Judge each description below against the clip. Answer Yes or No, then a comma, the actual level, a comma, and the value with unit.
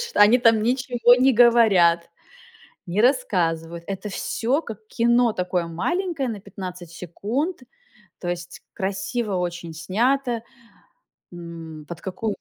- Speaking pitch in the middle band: No, high, 205 Hz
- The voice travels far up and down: Yes, wide, 5.8 semitones